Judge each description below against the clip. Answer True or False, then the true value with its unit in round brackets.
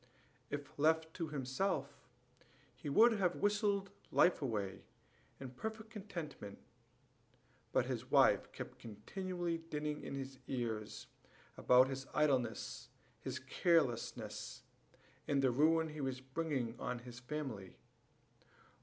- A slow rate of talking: True (115 wpm)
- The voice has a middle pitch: True (145 Hz)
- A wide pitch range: False (4.6 semitones)